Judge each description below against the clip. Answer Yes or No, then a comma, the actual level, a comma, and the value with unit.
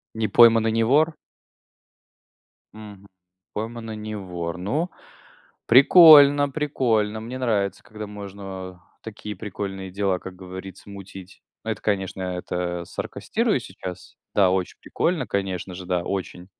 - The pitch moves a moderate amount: Yes, average, 3.2 semitones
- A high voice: No, low, 100 Hz